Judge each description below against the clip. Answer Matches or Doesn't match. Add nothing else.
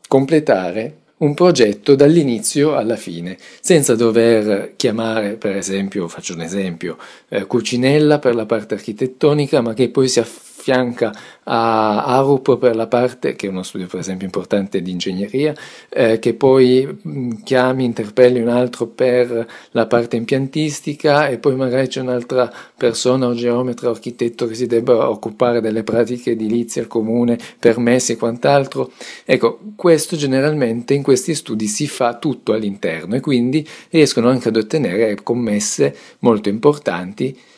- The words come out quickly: Doesn't match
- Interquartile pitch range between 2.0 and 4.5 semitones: Matches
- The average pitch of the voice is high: Doesn't match